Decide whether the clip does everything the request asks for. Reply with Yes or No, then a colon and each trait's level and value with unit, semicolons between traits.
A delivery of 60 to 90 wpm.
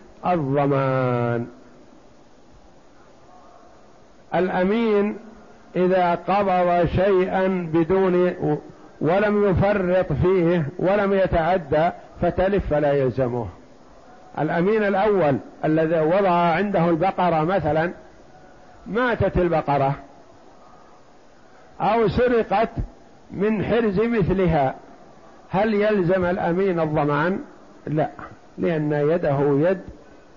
Yes: average, 70 wpm